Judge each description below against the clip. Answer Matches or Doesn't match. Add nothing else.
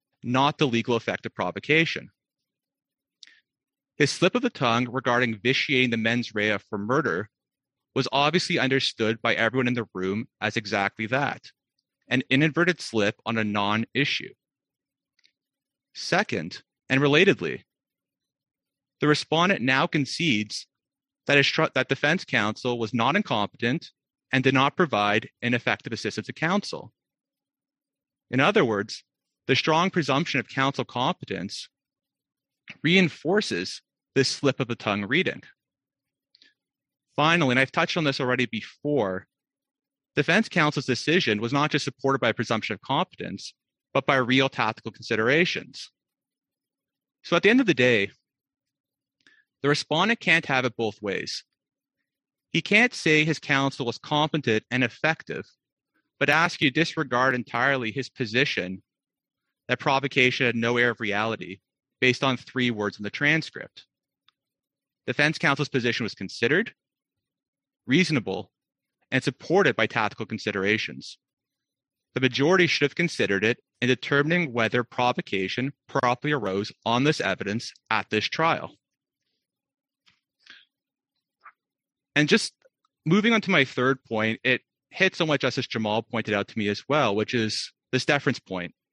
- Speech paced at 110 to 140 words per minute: Matches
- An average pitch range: Matches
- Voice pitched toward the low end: Matches